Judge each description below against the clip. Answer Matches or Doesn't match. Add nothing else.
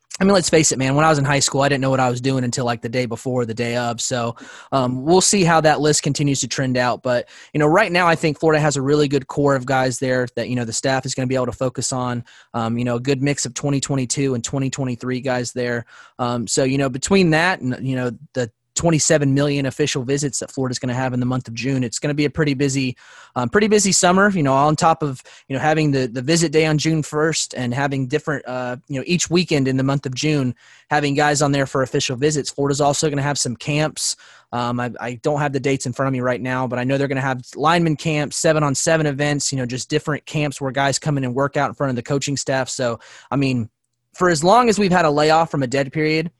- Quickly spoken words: Matches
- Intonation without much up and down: Doesn't match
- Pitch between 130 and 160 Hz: Matches